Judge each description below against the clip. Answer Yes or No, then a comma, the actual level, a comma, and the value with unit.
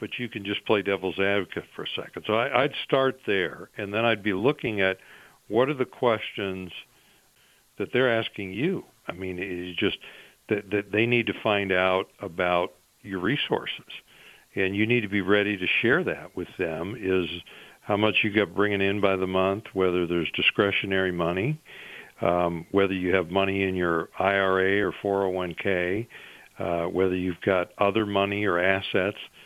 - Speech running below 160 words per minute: No, average, 180 wpm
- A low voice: Yes, very low, 95 Hz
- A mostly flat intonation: Yes, narrow, 2.0 semitones